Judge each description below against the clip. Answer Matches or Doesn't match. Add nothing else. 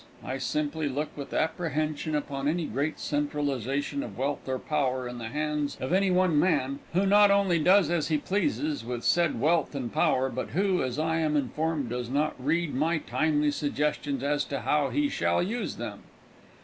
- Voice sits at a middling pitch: Matches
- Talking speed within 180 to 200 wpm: Matches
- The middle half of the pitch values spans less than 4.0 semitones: Matches